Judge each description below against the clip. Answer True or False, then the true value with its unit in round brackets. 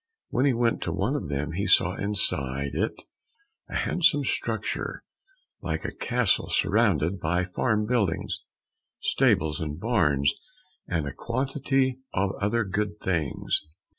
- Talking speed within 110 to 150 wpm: True (135 wpm)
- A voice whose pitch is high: False (100 Hz)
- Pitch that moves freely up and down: True (6.7 semitones)